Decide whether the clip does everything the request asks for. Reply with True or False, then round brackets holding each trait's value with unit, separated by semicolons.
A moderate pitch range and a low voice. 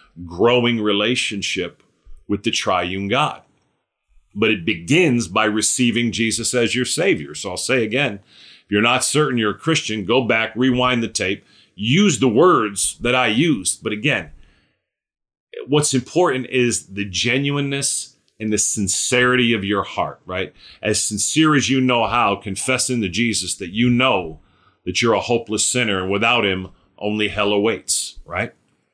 True (3.8 semitones; 115 Hz)